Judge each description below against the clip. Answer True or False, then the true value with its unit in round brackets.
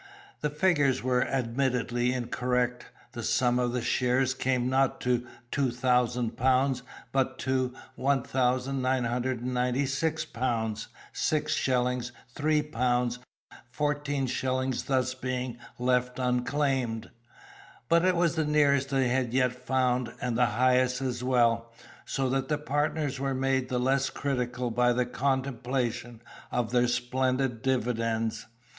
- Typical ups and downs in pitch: False (1.5 semitones)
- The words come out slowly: True (125 wpm)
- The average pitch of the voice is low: True (125 Hz)